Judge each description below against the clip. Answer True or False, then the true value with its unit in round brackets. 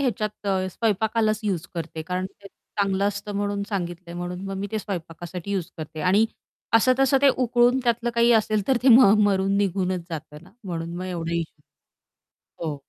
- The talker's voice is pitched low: False (195 Hz)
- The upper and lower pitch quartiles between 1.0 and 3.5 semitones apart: False (4.0 semitones)